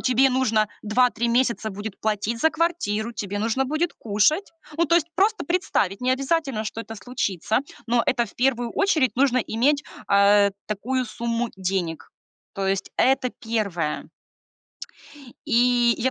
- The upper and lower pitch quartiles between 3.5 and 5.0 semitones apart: Yes, average, 4.0 semitones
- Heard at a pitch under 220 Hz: No, high, 235 Hz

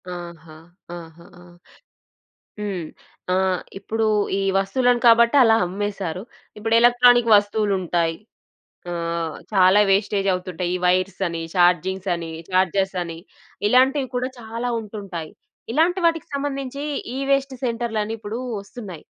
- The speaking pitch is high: Yes, high, 200 Hz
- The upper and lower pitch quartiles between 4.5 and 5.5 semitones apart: Yes, average, 4.9 semitones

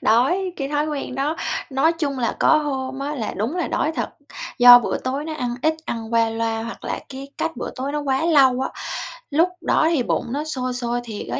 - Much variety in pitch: No, average, 3.8 semitones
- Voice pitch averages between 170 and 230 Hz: No, very high, 270 Hz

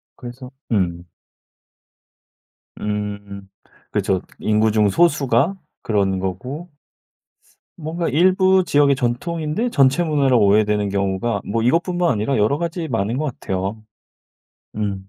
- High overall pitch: No, low, 120 Hz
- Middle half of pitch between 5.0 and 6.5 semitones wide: No, wide, 7.3 semitones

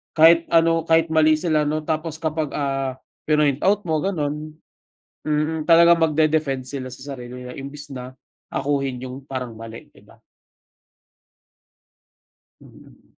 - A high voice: No, medium, 150 Hz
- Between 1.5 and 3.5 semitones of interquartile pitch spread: Yes, average, 2.8 semitones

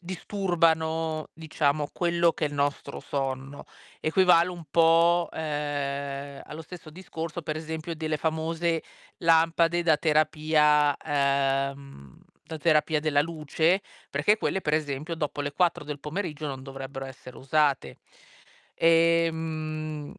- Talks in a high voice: No, medium, 155 Hz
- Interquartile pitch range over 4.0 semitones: No, narrow, 2.5 semitones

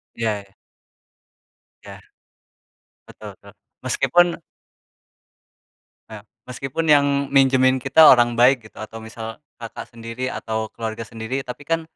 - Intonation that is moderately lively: Yes, average, 3.2 semitones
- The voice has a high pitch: No, low, 120 Hz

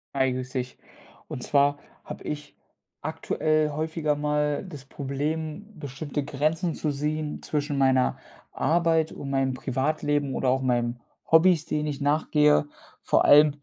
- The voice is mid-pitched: Yes, medium, 145 Hz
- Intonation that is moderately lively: No, narrow, 2.3 semitones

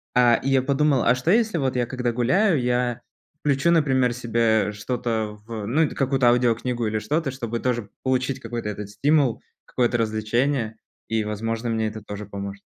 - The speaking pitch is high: No, low, 120 Hz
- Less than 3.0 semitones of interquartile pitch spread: No, average, 3.3 semitones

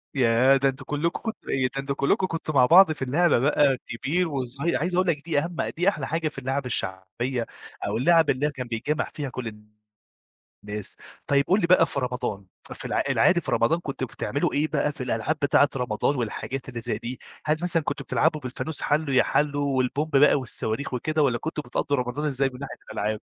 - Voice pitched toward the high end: No, medium, 140 Hz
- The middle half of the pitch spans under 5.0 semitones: Yes, average, 3.6 semitones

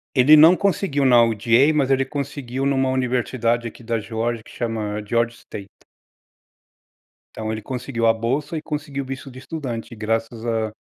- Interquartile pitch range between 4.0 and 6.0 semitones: No, average, 3.3 semitones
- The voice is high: No, low, 120 Hz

